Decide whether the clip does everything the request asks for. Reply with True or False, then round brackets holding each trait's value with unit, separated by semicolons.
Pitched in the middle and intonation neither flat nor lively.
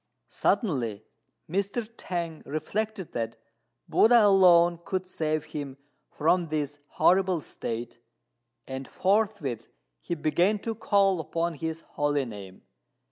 True (165 Hz; 5.0 semitones)